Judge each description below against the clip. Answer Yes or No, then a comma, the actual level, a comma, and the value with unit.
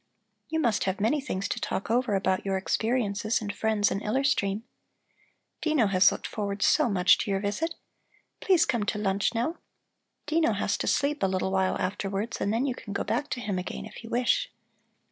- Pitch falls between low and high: No, high, 210 Hz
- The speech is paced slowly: No, average, 200 wpm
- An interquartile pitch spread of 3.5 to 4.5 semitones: Yes, average, 4.0 semitones